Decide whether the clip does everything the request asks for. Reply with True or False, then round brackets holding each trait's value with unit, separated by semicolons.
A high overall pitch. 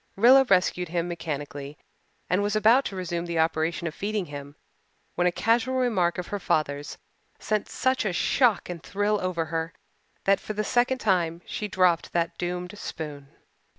False (180 Hz)